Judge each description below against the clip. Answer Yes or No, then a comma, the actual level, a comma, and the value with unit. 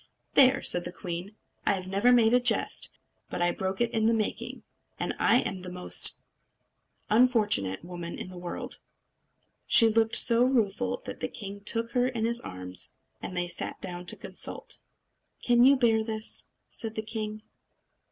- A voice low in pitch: No, high, 220 Hz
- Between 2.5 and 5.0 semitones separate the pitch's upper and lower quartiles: Yes, average, 4.5 semitones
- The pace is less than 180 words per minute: Yes, average, 165 wpm